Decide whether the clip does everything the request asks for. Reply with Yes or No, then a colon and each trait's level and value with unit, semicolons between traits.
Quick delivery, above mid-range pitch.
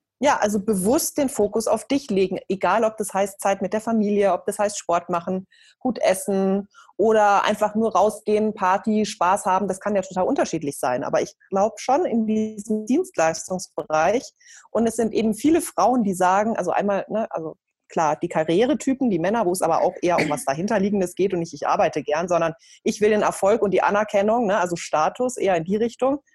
Yes: fast, 205 wpm; high, 205 Hz